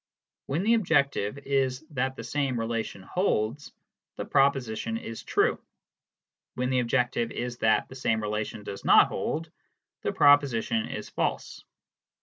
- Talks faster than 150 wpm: No, average, 140 wpm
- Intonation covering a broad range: No, average, 3.7 semitones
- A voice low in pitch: Yes, low, 125 Hz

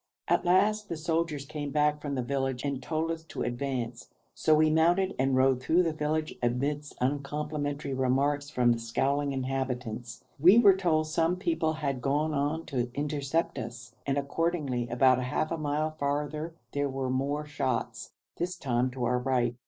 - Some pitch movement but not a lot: Yes, average, 3.2 semitones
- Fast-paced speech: No, average, 170 wpm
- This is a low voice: No, medium, 145 Hz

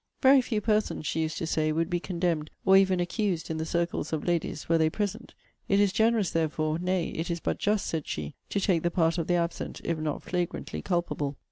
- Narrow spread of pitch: No, average, 3.3 semitones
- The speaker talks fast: Yes, fast, 225 wpm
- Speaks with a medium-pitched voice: Yes, medium, 170 Hz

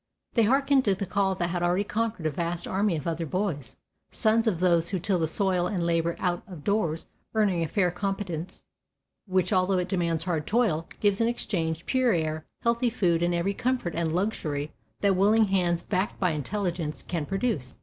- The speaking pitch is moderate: Yes, medium, 180 Hz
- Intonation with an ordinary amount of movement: Yes, average, 3.5 semitones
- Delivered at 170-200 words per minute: Yes, average, 190 wpm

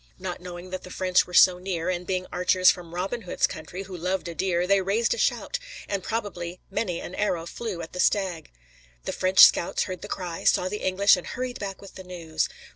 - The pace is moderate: No, fast, 220 wpm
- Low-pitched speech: No, medium, 185 Hz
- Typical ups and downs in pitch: No, narrow, 1.7 semitones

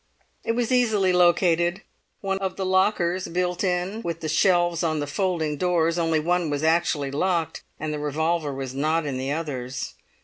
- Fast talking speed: No, average, 170 wpm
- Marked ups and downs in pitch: No, average, 3.2 semitones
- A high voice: No, medium, 170 Hz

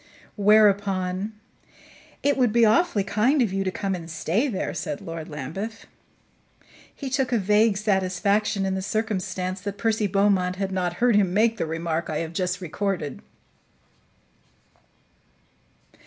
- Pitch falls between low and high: No, high, 195 Hz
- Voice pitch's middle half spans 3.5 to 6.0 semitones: No, average, 3.0 semitones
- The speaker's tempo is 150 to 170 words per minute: No, average, 140 wpm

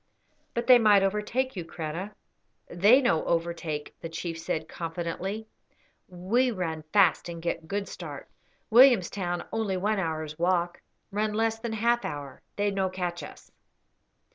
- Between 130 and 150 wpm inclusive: Yes, average, 140 wpm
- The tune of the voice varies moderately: Yes, average, 4.3 semitones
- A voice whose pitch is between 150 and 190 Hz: Yes, medium, 185 Hz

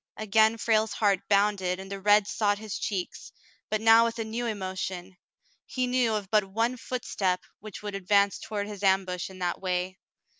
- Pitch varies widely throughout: No, narrow, 2.4 semitones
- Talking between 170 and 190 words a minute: Yes, average, 185 wpm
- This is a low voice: No, high, 205 Hz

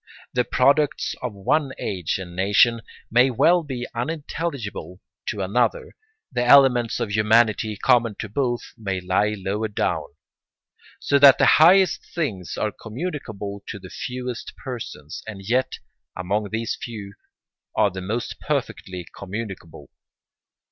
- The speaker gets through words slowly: Yes, slow, 130 wpm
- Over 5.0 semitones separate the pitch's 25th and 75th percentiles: No, average, 4.3 semitones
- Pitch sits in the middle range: No, low, 110 Hz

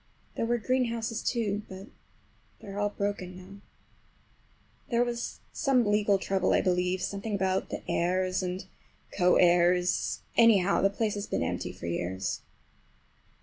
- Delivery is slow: No, average, 145 wpm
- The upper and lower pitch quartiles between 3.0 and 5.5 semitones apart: Yes, average, 3.3 semitones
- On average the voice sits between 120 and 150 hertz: No, high, 195 Hz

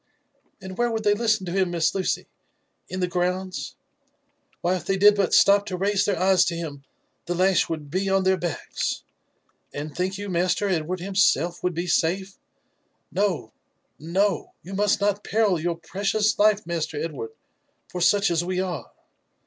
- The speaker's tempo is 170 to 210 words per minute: Yes, average, 180 wpm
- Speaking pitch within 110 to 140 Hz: No, medium, 185 Hz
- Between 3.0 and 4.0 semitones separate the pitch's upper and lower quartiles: No, narrow, 2.6 semitones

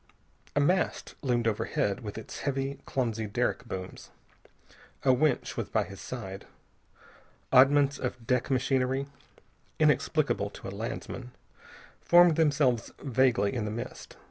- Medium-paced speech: No, slow, 125 wpm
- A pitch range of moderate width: Yes, average, 3.4 semitones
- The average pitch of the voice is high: No, low, 125 Hz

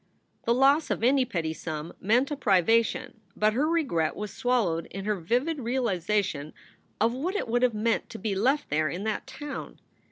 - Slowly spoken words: No, average, 185 wpm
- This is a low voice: No, high, 225 Hz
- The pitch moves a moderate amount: No, wide, 5.7 semitones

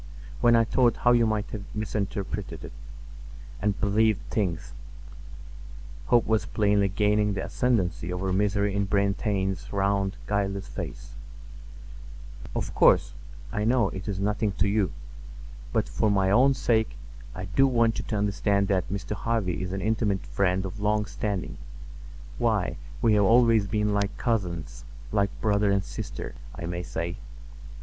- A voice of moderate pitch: No, low, 100 Hz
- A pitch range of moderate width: No, narrow, 2.2 semitones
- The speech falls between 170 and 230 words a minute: No, average, 140 wpm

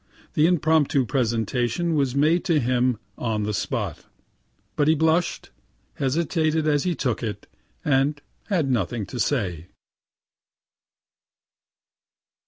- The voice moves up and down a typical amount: Yes, average, 5.0 semitones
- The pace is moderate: No, slow, 110 wpm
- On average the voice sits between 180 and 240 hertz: No, medium, 140 Hz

